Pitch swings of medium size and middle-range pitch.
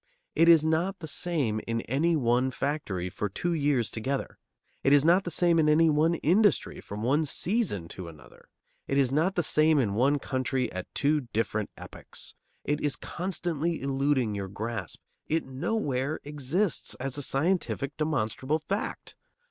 Yes: average, 4.8 semitones; medium, 145 Hz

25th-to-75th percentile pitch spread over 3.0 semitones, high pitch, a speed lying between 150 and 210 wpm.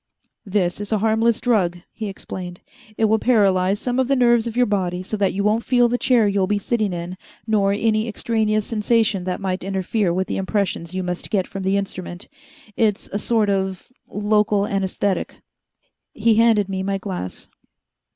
No: average, 2.7 semitones; high, 205 Hz; average, 180 wpm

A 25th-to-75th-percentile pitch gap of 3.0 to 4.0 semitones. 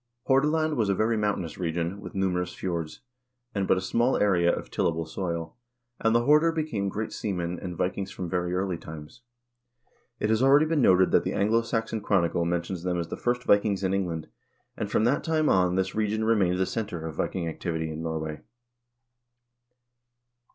No: average, 4.4 semitones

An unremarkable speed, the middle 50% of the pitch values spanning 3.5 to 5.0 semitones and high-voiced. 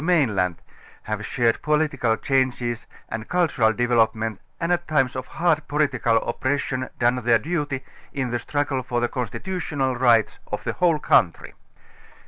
No: average, 145 wpm; average, 4.4 semitones; low, 130 Hz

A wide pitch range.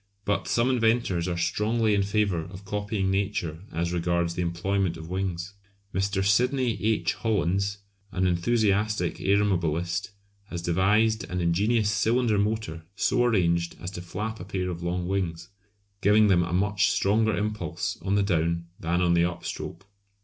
No: average, 3.4 semitones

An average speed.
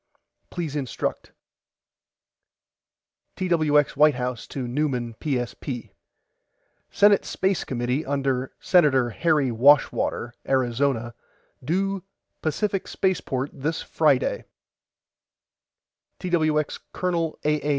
No: slow, 85 wpm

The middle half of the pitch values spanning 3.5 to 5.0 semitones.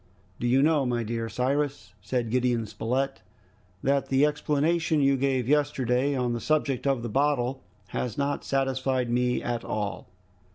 No: narrow, 2.6 semitones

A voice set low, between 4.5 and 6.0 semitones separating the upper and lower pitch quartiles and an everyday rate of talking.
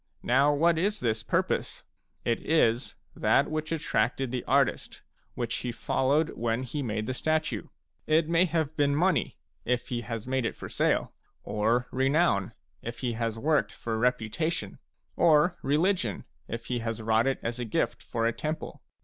Yes: low, 125 Hz; average, 5.2 semitones; average, 165 wpm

